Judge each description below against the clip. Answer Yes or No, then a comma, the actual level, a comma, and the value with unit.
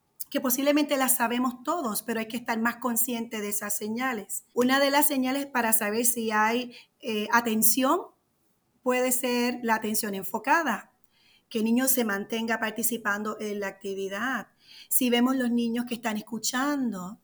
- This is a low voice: No, high, 235 Hz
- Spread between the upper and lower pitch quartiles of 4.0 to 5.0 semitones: No, average, 2.7 semitones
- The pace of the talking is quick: No, average, 155 wpm